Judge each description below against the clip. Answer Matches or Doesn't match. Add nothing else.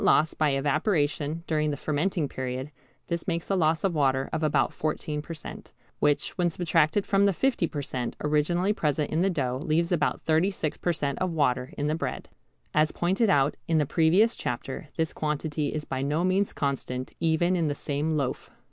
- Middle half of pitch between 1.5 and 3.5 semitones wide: Matches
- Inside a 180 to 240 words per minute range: Matches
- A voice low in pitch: Doesn't match